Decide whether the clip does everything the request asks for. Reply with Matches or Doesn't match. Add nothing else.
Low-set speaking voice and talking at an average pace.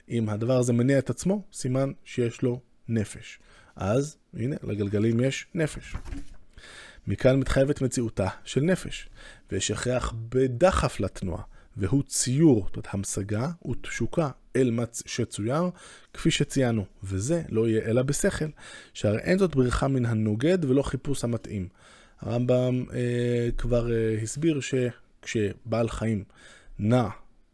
Matches